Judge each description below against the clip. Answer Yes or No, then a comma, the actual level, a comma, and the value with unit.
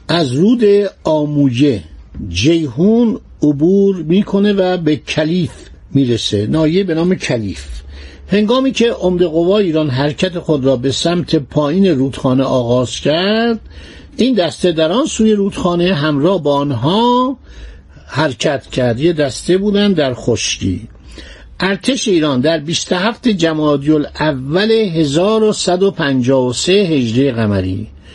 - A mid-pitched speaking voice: Yes, medium, 160 Hz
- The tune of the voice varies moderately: No, wide, 6.7 semitones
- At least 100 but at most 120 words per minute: Yes, average, 115 wpm